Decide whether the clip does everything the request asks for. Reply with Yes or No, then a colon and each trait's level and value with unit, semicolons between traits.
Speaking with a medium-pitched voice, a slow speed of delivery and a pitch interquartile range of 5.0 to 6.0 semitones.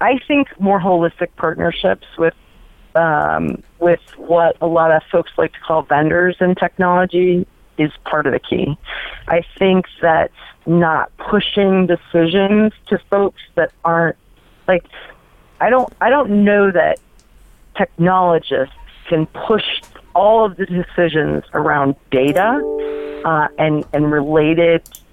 No: medium, 170 Hz; slow, 130 wpm; average, 3.1 semitones